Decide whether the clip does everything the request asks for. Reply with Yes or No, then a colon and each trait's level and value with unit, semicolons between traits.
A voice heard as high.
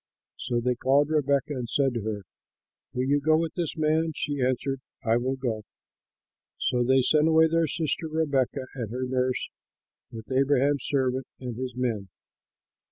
No: low, 130 Hz